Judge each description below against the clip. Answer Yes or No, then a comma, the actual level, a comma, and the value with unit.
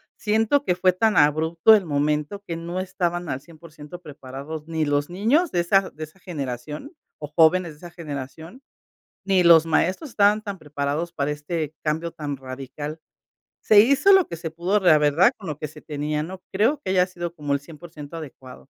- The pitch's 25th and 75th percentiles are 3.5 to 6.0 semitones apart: Yes, average, 3.8 semitones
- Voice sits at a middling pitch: Yes, medium, 165 Hz